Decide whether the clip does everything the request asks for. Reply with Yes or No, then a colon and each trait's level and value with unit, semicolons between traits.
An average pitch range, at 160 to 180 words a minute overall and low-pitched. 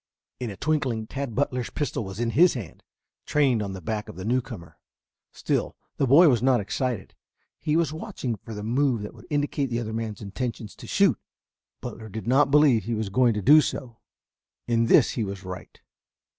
No: average, 4.4 semitones; average, 195 wpm; low, 120 Hz